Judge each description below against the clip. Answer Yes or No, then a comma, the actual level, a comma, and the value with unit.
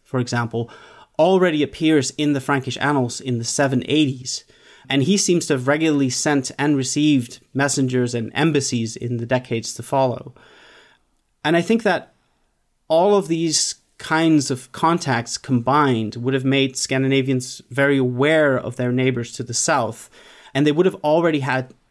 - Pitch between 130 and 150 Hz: Yes, low, 135 Hz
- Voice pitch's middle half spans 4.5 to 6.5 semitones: No, average, 2.9 semitones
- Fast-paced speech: No, average, 155 wpm